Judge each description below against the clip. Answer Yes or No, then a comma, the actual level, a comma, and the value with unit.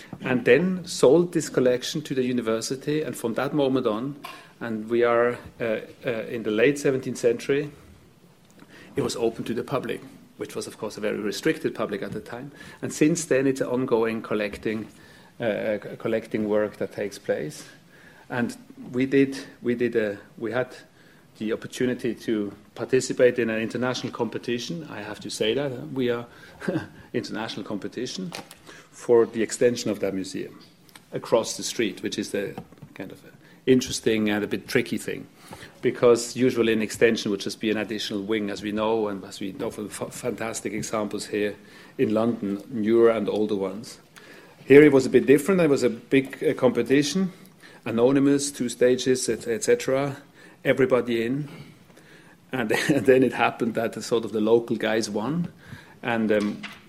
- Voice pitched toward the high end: No, low, 120 Hz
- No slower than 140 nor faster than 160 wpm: No, average, 170 wpm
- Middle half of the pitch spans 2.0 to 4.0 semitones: Yes, average, 3.5 semitones